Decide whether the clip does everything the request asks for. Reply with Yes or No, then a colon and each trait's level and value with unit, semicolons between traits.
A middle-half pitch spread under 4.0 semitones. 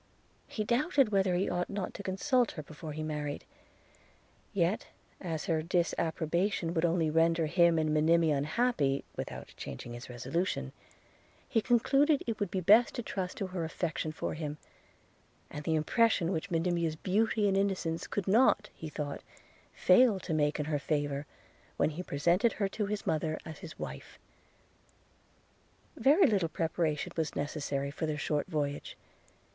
No: average, 4.5 semitones